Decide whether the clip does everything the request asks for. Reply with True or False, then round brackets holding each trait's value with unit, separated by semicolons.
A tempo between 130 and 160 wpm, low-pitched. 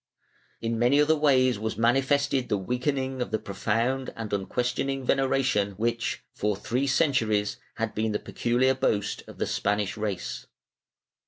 True (145 wpm; 120 Hz)